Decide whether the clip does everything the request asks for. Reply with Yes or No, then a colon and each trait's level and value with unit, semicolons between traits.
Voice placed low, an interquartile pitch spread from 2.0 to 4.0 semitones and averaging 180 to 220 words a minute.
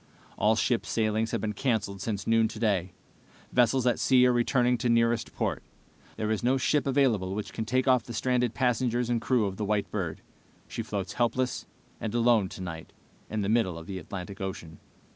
Yes: low, 110 Hz; average, 3.6 semitones; average, 190 wpm